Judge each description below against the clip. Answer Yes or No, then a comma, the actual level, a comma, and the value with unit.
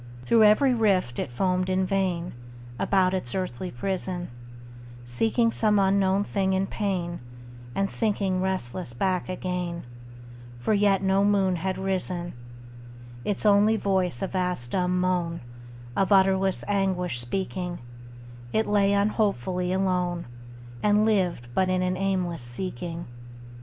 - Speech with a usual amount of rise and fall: No, narrow, 1.7 semitones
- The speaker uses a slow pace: Yes, slow, 125 wpm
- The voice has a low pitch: No, medium, 185 Hz